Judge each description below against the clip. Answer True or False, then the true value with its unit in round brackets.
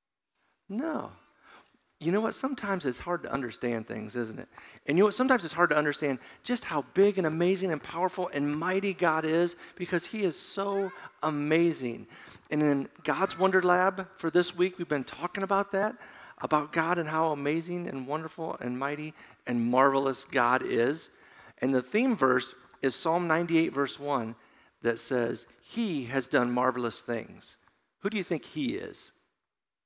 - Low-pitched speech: False (160 Hz)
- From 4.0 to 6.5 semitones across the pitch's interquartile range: True (5.6 semitones)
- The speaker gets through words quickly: False (170 wpm)